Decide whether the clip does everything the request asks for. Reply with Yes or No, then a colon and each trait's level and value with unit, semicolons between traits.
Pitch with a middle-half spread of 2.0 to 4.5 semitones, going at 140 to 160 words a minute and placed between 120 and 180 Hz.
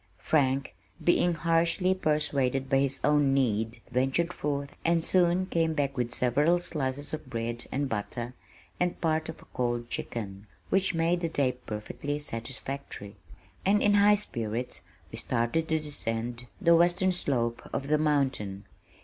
No: average, 5.3 semitones; average, 150 wpm; medium, 140 Hz